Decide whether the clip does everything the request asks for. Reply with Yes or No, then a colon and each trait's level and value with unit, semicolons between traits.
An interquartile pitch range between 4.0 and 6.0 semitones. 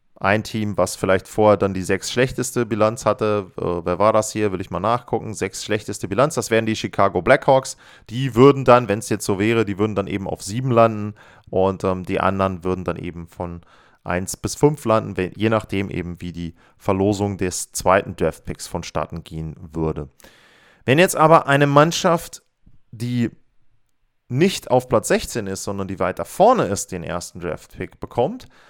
Yes: average, 4.4 semitones